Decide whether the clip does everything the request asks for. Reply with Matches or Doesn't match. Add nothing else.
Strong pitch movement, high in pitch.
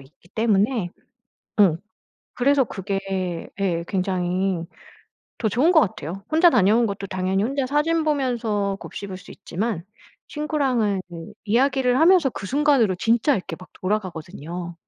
Matches